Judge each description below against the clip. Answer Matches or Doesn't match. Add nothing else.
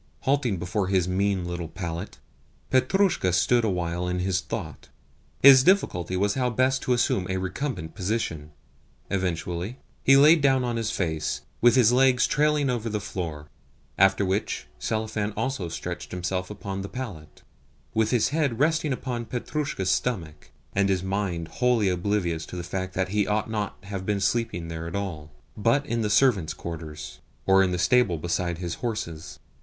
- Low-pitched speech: Matches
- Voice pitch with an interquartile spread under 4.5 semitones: Doesn't match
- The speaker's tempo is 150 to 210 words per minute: Matches